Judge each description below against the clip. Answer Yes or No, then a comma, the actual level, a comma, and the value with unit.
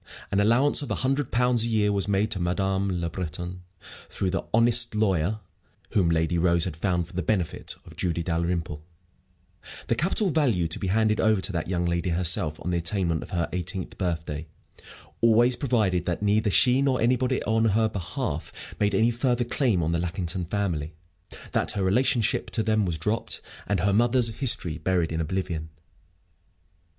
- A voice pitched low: Yes, very low, 95 Hz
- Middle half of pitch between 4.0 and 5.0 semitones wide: Yes, average, 4.7 semitones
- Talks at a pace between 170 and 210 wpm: Yes, average, 180 wpm